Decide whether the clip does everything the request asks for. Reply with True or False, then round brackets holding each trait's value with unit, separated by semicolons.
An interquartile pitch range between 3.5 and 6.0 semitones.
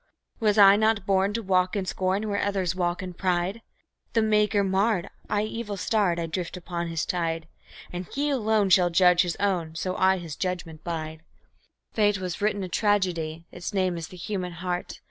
False (2.8 semitones)